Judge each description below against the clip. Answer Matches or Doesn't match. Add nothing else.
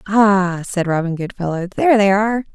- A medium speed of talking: Matches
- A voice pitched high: Matches